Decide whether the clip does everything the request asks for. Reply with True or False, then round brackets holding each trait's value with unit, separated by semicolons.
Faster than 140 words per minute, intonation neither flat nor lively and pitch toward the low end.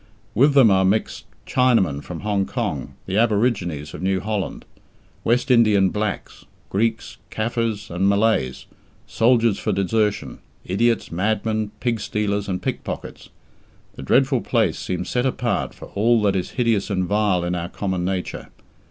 True (150 wpm; 3.5 semitones; 105 Hz)